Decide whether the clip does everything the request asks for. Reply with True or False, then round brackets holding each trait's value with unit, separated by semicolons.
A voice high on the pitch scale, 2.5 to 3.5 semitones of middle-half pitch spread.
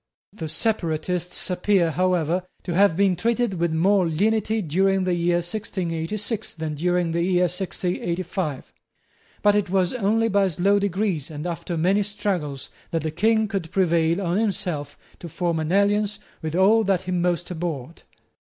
False (180 Hz; 3.2 semitones)